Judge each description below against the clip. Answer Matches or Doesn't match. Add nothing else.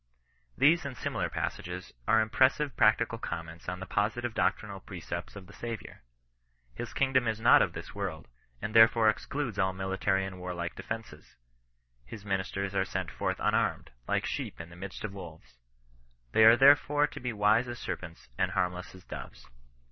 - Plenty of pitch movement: Doesn't match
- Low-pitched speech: Matches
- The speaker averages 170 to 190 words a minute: Matches